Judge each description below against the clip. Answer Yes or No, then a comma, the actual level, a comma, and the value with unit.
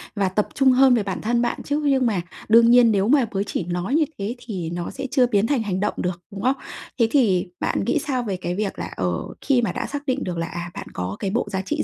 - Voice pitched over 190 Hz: Yes, high, 215 Hz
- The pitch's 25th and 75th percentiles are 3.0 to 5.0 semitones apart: No, wide, 5.5 semitones